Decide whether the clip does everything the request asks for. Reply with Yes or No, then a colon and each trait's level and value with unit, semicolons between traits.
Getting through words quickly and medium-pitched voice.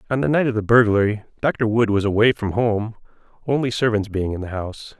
No: fast, 215 wpm; low, 110 Hz